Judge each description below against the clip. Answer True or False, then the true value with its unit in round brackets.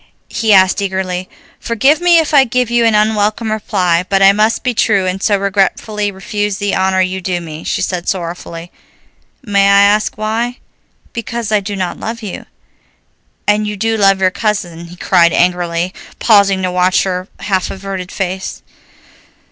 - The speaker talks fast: False (170 wpm)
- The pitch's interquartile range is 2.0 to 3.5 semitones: True (2.7 semitones)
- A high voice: True (195 Hz)